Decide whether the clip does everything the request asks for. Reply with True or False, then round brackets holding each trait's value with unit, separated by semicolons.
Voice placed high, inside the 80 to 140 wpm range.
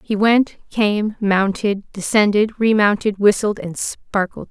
True (205 Hz; 135 wpm)